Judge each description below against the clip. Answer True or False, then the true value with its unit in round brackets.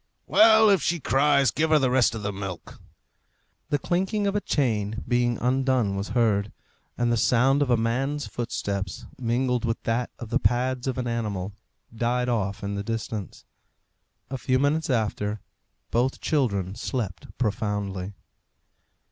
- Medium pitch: False (120 Hz)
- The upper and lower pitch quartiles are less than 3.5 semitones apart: False (4.2 semitones)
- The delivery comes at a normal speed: True (155 wpm)